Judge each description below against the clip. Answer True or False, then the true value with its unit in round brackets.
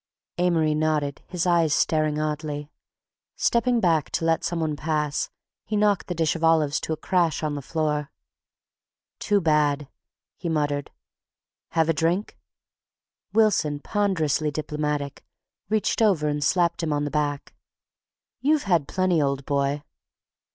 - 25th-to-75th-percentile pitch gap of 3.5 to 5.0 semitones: False (2.8 semitones)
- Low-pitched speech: False (155 Hz)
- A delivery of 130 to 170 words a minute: True (140 wpm)